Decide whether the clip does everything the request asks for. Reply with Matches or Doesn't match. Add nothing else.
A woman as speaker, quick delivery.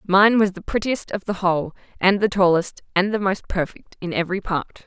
Matches